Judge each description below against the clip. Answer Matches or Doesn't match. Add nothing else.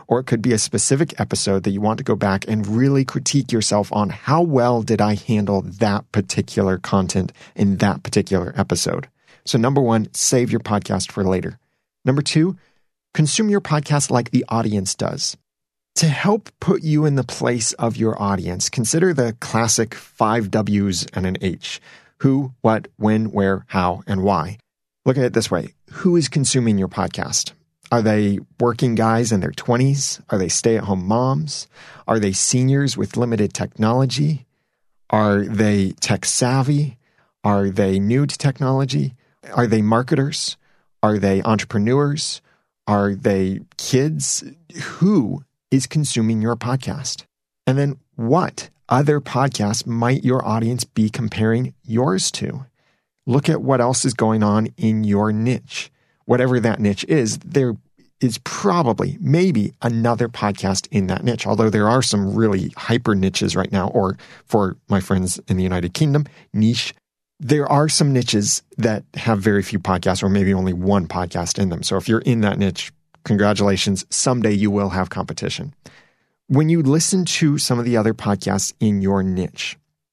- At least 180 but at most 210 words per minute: Doesn't match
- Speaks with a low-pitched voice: Matches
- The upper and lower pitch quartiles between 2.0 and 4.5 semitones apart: Doesn't match